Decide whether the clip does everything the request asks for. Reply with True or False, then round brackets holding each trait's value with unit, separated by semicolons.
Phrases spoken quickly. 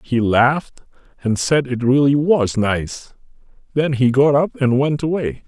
False (165 wpm)